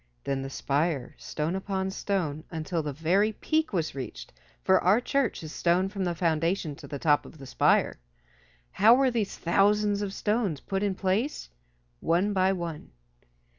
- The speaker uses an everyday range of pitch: Yes, average, 4.5 semitones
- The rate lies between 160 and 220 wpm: Yes, average, 170 wpm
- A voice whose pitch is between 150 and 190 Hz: Yes, medium, 185 Hz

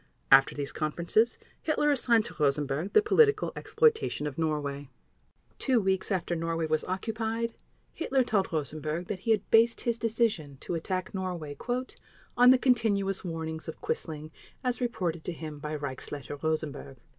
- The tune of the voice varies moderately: No, wide, 7.0 semitones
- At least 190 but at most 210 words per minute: No, average, 150 wpm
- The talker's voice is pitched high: No, medium, 175 Hz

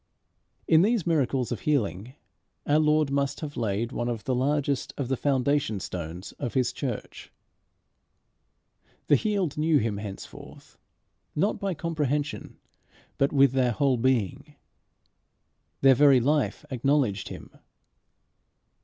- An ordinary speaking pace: No, slow, 125 wpm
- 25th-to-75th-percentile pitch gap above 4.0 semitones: No, average, 3.7 semitones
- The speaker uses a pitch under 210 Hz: Yes, low, 135 Hz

